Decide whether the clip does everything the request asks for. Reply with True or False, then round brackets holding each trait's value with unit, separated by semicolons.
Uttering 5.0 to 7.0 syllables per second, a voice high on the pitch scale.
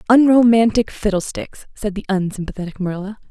True (5.8 syllables/s; 205 Hz)